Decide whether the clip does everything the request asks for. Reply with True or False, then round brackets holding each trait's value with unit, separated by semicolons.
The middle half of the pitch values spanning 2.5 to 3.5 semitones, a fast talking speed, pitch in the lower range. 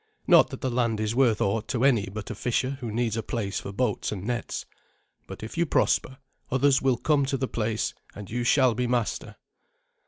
True (3.2 semitones; 210 wpm; 120 Hz)